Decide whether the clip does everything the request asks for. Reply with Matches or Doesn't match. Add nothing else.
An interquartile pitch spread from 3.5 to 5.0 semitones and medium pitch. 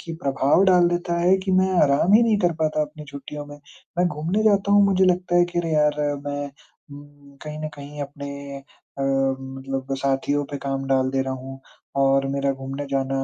Matches